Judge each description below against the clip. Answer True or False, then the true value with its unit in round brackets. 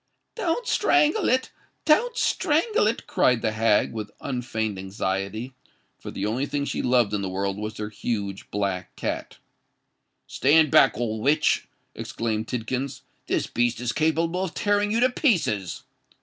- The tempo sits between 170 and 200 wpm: False (145 wpm)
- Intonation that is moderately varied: False (8.1 semitones)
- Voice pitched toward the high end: False (120 Hz)